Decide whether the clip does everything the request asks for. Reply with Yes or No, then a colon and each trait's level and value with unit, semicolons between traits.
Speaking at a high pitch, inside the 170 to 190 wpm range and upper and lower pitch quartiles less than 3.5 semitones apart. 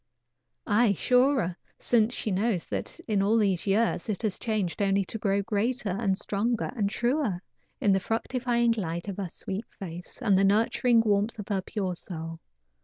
Yes: high, 205 Hz; average, 175 wpm; average, 3.1 semitones